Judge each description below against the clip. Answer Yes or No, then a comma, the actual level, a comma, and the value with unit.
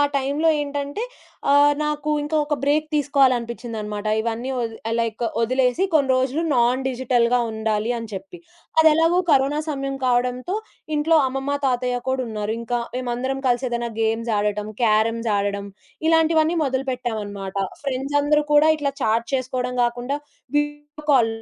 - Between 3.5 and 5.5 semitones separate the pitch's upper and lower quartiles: Yes, average, 3.8 semitones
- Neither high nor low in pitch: No, very high, 255 Hz